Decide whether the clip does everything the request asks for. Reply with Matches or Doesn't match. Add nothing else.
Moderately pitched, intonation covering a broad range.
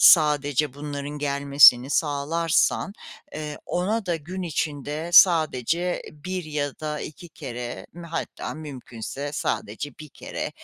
Doesn't match